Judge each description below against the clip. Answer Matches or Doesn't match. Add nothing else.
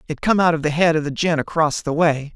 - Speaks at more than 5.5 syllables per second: Matches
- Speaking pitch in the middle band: Matches